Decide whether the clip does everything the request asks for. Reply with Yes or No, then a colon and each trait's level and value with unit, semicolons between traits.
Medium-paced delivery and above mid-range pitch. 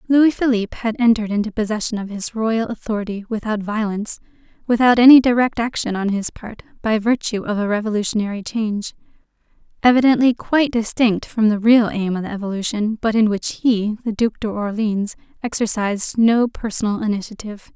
Yes: average, 155 wpm; high, 220 Hz